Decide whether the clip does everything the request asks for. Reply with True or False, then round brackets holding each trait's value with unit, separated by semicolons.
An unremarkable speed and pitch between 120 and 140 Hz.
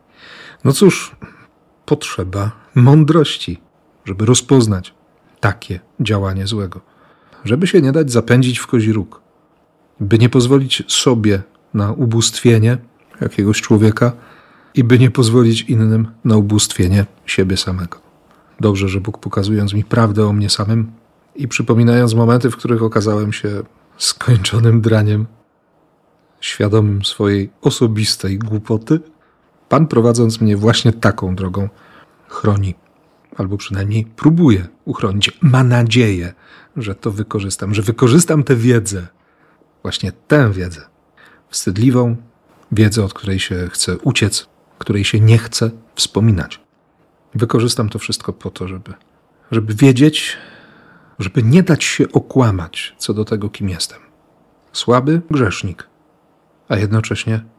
False (120 wpm; 110 Hz)